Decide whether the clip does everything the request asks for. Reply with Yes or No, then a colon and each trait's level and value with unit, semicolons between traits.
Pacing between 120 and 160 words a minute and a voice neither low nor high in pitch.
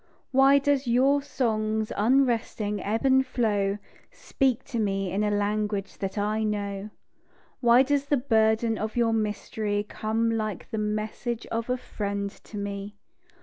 No: average, 150 wpm; high, 220 Hz